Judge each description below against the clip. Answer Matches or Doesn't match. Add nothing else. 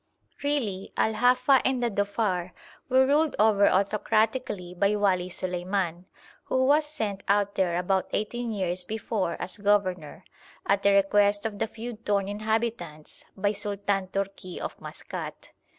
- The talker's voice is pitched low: Doesn't match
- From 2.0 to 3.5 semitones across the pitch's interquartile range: Matches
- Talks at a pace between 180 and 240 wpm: Doesn't match